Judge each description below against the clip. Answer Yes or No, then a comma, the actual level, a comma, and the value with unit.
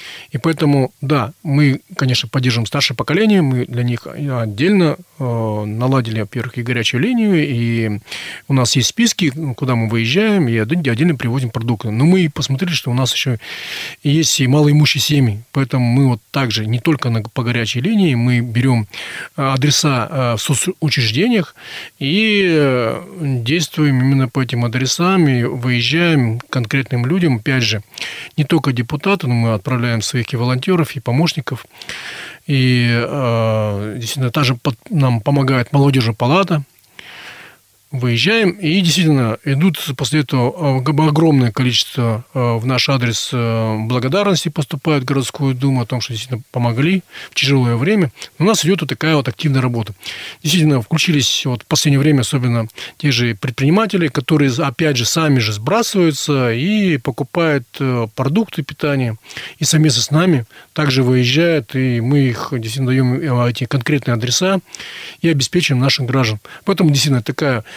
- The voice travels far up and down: No, average, 4.1 semitones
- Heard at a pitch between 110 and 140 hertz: Yes, low, 135 Hz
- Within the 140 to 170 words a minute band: Yes, average, 145 wpm